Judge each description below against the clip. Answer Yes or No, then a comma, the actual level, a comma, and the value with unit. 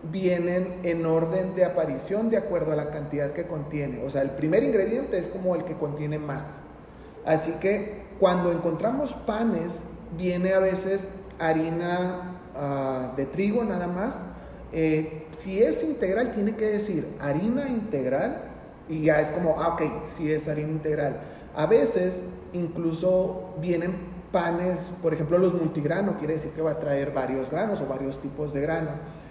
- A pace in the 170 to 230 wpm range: No, average, 160 wpm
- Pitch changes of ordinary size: Yes, average, 3.2 semitones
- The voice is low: No, medium, 165 Hz